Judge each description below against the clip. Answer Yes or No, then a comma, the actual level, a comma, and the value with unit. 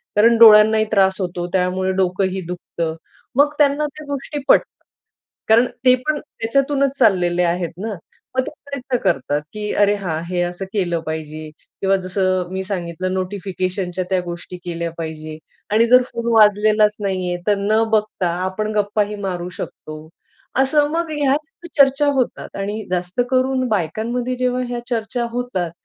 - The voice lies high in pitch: Yes, high, 205 Hz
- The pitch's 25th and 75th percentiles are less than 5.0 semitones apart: No, average, 5.3 semitones